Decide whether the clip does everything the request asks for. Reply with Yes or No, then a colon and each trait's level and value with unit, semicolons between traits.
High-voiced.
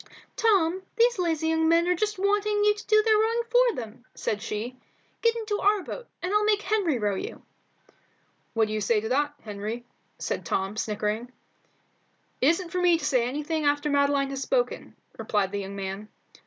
Yes: very high, 320 Hz